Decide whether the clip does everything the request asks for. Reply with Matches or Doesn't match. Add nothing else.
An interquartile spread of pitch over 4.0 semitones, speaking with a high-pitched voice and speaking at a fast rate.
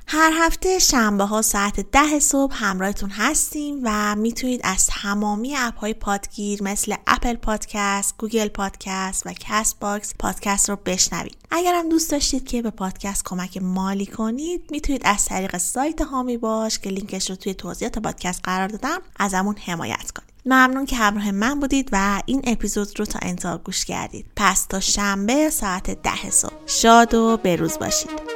Matches